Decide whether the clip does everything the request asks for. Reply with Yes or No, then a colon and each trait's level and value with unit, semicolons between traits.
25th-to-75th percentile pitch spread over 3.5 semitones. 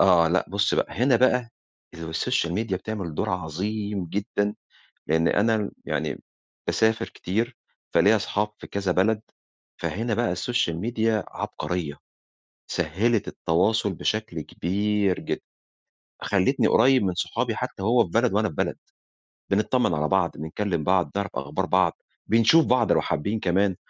Yes: average, 4.0 semitones